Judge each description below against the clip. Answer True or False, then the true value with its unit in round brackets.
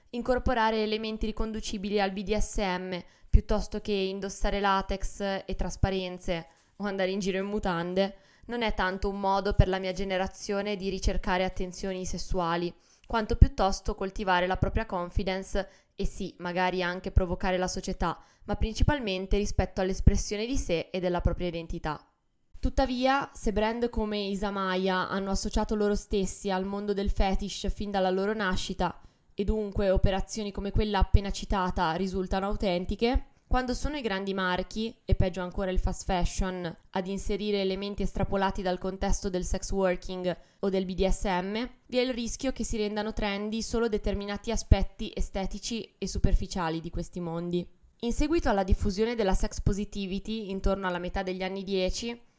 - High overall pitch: True (195 Hz)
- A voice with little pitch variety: True (2.2 semitones)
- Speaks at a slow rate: False (150 wpm)